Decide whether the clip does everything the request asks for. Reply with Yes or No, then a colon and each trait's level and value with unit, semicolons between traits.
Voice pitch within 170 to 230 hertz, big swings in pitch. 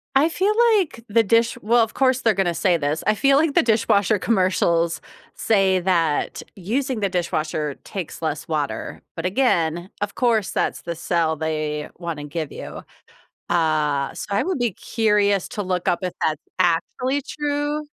Yes: high, 190 Hz; wide, 6.0 semitones